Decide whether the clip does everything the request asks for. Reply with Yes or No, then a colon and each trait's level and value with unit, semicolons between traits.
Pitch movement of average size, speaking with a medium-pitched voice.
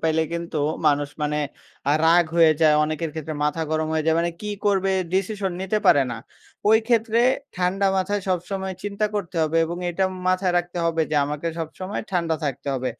Yes: average, 3.5 semitones; medium, 170 Hz